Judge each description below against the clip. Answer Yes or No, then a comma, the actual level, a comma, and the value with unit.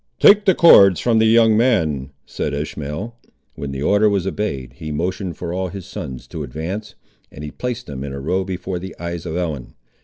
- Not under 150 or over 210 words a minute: Yes, fast, 205 wpm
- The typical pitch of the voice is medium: No, very low, 90 Hz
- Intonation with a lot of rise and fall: Yes, wide, 6.0 semitones